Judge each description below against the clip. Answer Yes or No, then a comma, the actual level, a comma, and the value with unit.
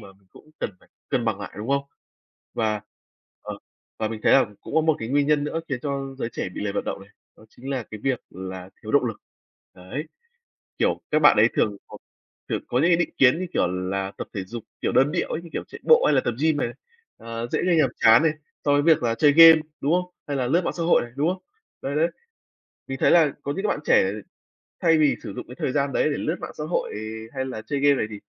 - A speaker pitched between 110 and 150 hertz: Yes, low, 135 Hz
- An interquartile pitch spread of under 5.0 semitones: No, wide, 5.6 semitones